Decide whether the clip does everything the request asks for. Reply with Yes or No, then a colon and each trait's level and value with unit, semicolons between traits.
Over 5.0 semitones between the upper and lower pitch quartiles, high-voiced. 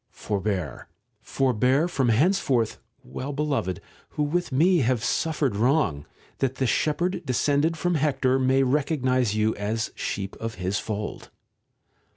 No: wide, 5.4 semitones; low, 130 Hz